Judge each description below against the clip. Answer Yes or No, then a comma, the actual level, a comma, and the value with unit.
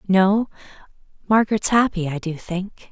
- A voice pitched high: Yes, high, 195 Hz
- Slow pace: Yes, slow, 125 wpm